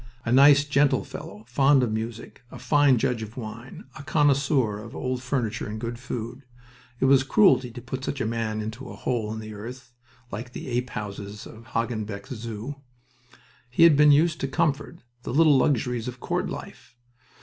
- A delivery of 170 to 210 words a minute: Yes, average, 180 wpm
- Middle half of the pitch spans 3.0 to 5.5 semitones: Yes, average, 3.8 semitones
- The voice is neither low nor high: No, low, 125 Hz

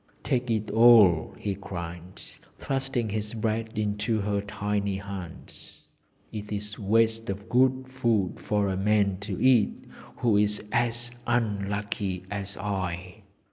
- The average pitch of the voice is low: Yes, low, 105 Hz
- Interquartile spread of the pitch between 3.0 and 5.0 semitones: No, narrow, 2.4 semitones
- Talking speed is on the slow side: Yes, slow, 130 wpm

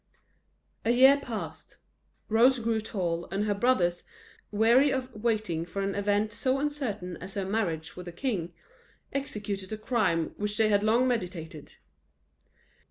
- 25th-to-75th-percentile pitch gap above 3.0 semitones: Yes, average, 4.6 semitones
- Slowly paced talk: No, average, 145 wpm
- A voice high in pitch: Yes, high, 210 Hz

